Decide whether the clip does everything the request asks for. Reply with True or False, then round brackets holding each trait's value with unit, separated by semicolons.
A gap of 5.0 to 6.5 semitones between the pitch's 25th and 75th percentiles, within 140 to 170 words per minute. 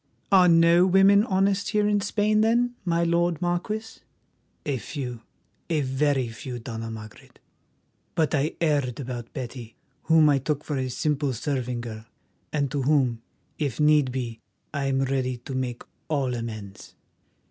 True (5.4 semitones; 150 wpm)